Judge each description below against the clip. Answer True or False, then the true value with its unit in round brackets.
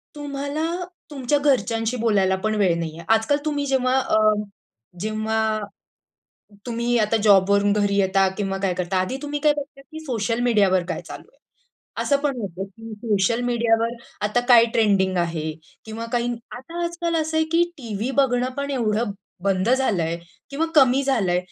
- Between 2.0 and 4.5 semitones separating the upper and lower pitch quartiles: False (5.3 semitones)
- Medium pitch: False (230 Hz)